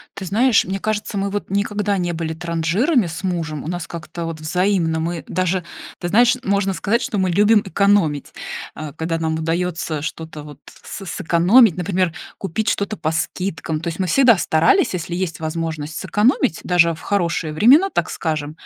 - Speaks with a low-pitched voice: No, medium, 175 Hz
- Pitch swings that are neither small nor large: Yes, average, 3.8 semitones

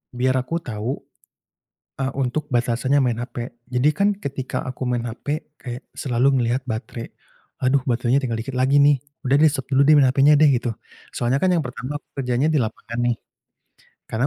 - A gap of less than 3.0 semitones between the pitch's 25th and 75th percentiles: Yes, narrow, 2.6 semitones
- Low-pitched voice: Yes, low, 130 Hz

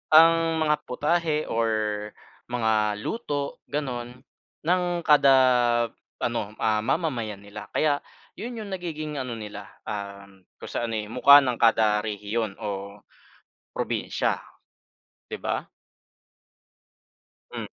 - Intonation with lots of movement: Yes, wide, 6.2 semitones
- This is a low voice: Yes, low, 120 Hz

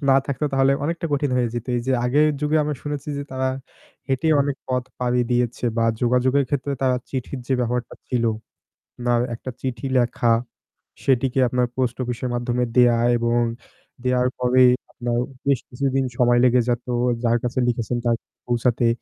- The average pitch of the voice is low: Yes, low, 125 Hz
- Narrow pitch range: Yes, narrow, 1.7 semitones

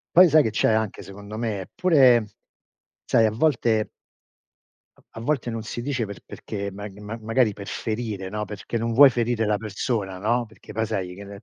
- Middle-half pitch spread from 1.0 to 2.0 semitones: No, narrow, 2.6 semitones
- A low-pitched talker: Yes, low, 110 Hz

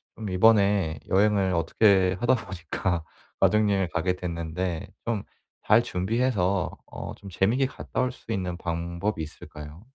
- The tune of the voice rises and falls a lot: No, average, 3.6 semitones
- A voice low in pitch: Yes, very low, 95 Hz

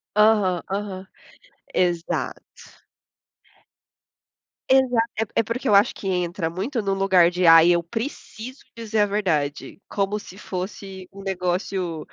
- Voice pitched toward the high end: Yes, high, 195 Hz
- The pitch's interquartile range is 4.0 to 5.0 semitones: No, average, 3.0 semitones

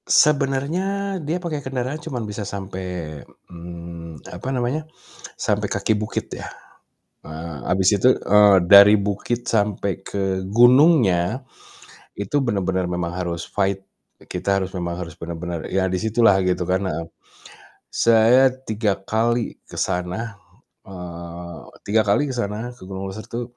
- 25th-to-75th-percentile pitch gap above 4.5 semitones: Yes, average, 5.2 semitones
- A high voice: No, low, 100 Hz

